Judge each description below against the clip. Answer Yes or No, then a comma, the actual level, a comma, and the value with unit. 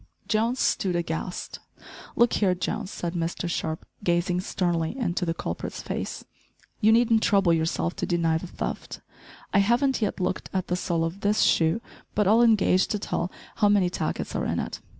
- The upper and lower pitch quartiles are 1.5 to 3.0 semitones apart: No, average, 3.8 semitones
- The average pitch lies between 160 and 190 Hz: Yes, medium, 185 Hz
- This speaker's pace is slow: No, average, 175 wpm